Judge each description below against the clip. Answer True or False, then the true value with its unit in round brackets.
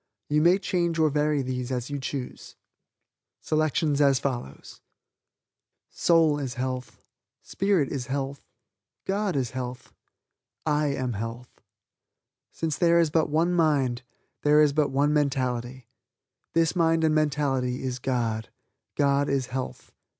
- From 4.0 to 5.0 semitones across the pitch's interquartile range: False (3.4 semitones)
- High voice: False (140 Hz)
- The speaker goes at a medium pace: False (120 wpm)